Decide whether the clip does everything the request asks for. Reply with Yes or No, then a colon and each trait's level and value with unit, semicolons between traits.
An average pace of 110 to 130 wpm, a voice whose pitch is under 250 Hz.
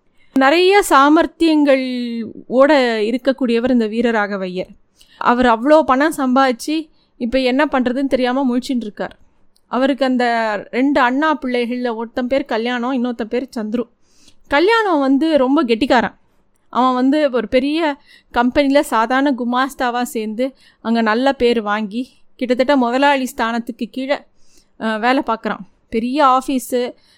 No: average, 115 wpm; very high, 255 Hz